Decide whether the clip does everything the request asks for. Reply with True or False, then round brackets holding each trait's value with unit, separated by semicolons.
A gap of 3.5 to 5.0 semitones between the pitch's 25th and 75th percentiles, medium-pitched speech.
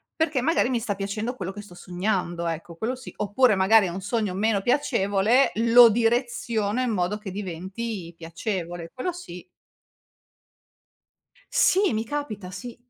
False (4.4 semitones; 210 Hz)